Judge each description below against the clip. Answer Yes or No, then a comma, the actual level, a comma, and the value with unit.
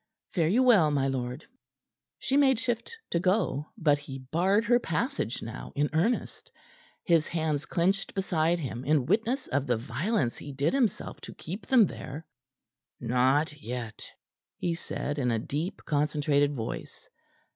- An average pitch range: No, wide, 6.3 semitones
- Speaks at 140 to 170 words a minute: Yes, average, 150 wpm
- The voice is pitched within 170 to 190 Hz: No, medium, 155 Hz